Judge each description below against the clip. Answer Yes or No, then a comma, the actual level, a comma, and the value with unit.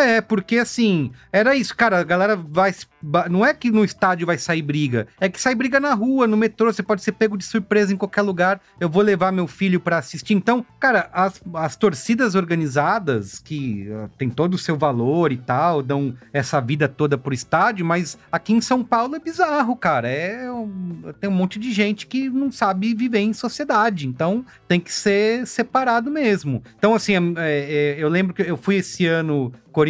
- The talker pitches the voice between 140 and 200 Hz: Yes, high, 190 Hz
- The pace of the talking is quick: Yes, fast, 200 wpm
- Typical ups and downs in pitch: No, wide, 6.1 semitones